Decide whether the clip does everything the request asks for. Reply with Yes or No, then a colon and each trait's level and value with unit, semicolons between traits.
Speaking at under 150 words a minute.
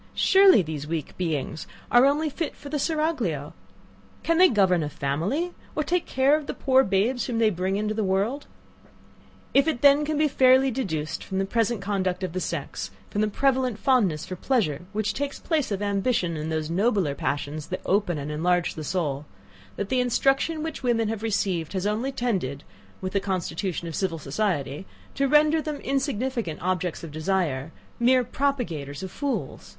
No: average, 180 wpm